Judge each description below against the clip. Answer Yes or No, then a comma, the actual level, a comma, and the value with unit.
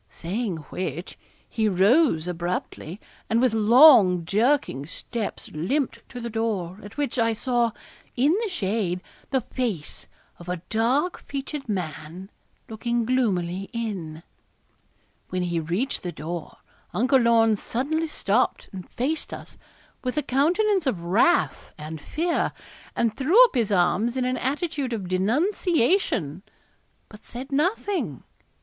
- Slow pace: Yes, slow, 130 wpm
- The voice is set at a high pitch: Yes, high, 225 Hz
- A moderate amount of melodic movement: No, wide, 6.8 semitones